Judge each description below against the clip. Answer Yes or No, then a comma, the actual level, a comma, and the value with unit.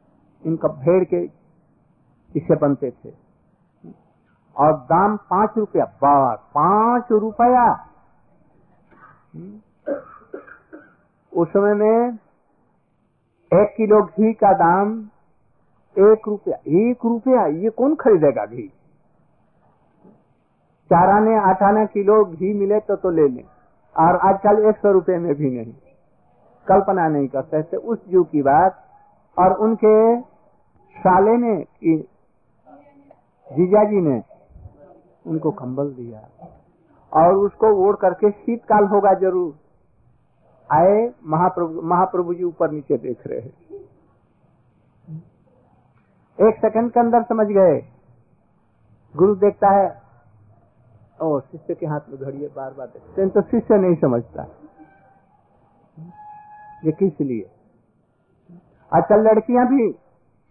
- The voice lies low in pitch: No, high, 190 Hz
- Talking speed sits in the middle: No, slow, 105 wpm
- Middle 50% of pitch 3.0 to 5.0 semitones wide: No, wide, 5.6 semitones